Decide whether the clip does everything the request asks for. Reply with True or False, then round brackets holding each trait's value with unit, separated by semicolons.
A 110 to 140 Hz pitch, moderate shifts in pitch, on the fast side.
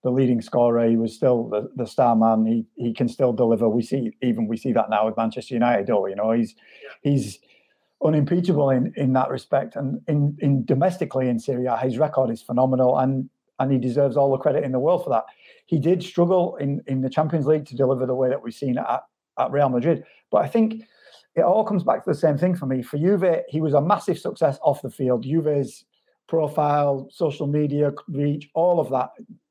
True (135 Hz; 4.0 semitones; 220 wpm)